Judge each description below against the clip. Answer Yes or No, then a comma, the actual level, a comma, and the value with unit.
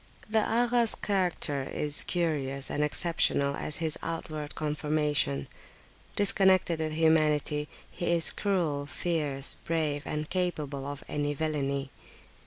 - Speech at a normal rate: No, slow, 115 wpm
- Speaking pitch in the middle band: Yes, medium, 155 Hz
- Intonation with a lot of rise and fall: No, average, 2.8 semitones